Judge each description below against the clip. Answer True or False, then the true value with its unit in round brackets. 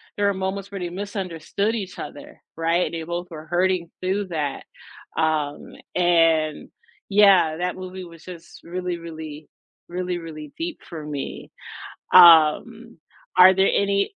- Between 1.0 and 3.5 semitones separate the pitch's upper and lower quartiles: True (3.1 semitones)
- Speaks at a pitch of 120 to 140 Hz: False (175 Hz)